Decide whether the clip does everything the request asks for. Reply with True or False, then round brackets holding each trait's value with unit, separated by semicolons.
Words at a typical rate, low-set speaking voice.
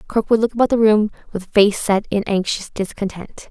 False (190 wpm; 205 Hz)